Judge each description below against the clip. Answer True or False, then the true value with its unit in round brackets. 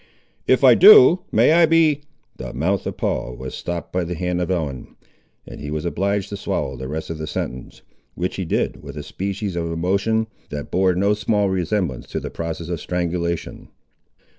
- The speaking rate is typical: True (190 wpm)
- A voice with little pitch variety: False (3.8 semitones)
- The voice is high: False (90 Hz)